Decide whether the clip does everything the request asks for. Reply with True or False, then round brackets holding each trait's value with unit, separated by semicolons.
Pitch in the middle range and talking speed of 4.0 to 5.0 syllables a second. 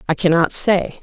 True (175 Hz; 4.8 syllables/s)